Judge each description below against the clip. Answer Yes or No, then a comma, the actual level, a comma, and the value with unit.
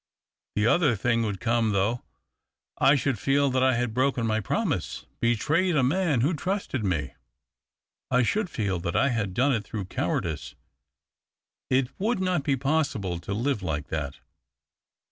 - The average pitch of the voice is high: No, low, 120 Hz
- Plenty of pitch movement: Yes, wide, 5.7 semitones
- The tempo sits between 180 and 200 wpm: No, average, 165 wpm